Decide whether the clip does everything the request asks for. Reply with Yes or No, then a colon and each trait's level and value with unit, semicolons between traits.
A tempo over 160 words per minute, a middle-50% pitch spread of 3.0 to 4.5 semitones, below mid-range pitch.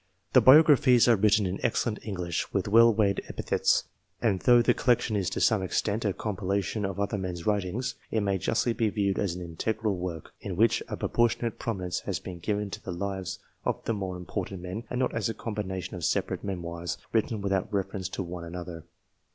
Yes: average, 200 wpm; average, 3.3 semitones; low, 100 Hz